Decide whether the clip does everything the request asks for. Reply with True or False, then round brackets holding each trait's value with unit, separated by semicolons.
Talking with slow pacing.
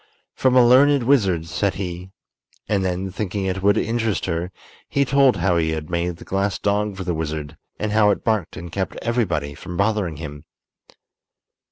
False (180 wpm)